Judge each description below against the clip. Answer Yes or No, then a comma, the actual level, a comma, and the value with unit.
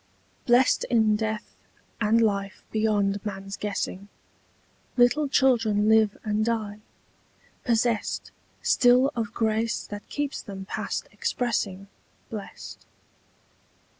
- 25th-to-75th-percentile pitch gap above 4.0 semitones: No, narrow, 2.4 semitones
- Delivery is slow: Yes, slow, 100 wpm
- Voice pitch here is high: Yes, high, 220 Hz